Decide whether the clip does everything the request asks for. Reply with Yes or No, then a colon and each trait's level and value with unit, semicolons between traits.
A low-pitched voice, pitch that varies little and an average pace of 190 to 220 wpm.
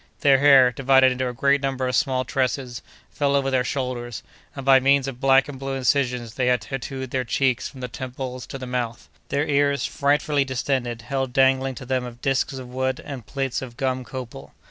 Yes: low, 130 Hz; narrow, 1.4 semitones; average, 200 wpm